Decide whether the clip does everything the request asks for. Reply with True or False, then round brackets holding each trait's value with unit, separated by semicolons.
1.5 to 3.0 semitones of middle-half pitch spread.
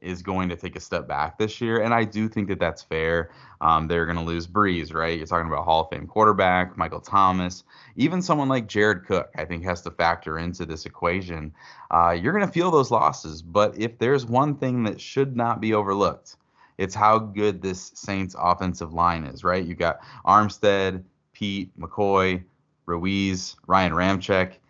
False (3.7 semitones)